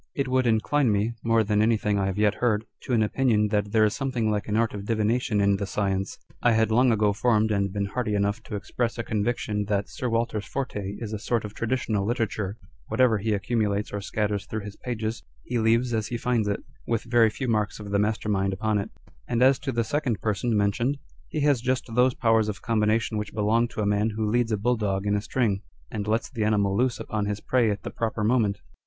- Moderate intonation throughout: No, narrow, 2.3 semitones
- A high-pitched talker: No, low, 110 Hz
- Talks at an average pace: No, fast, 235 wpm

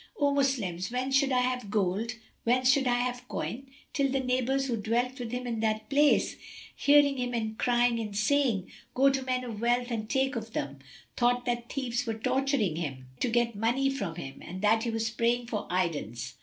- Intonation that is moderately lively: Yes, average, 3.0 semitones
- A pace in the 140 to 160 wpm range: No, average, 195 wpm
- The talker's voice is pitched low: No, high, 240 Hz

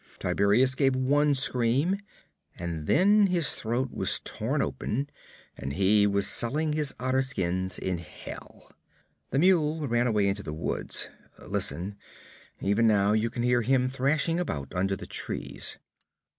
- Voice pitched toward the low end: Yes, low, 120 Hz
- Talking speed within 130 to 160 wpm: Yes, average, 145 wpm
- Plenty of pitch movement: Yes, wide, 6.0 semitones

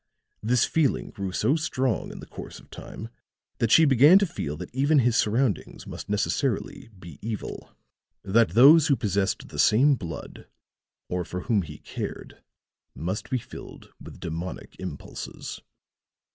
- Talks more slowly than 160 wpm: Yes, average, 150 wpm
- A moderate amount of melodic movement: No, wide, 6.2 semitones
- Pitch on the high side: No, low, 115 Hz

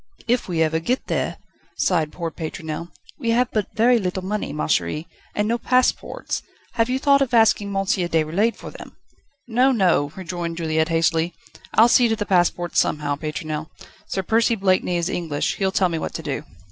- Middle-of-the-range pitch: Yes, medium, 180 Hz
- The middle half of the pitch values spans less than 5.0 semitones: No, wide, 5.6 semitones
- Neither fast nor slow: Yes, average, 185 wpm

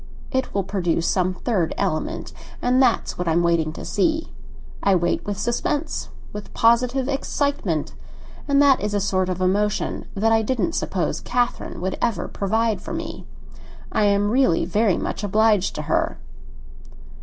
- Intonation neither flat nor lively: Yes, average, 4.7 semitones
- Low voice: No, high, 205 Hz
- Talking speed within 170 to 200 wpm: No, average, 155 wpm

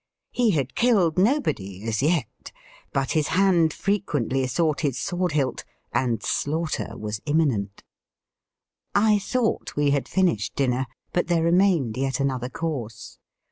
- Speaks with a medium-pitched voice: Yes, medium, 145 Hz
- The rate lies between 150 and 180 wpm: No, slow, 135 wpm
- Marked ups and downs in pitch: Yes, wide, 5.7 semitones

